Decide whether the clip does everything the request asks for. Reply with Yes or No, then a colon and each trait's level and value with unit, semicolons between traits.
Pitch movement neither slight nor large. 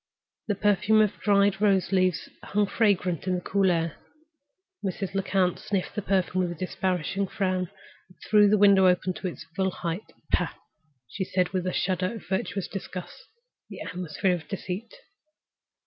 No: narrow, 1.7 semitones